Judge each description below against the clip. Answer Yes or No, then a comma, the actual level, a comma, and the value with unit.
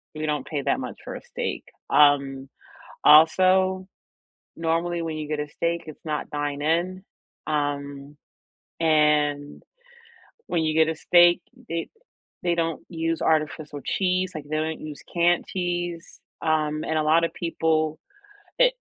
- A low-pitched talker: No, medium, 160 Hz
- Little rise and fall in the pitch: Yes, narrow, 2.2 semitones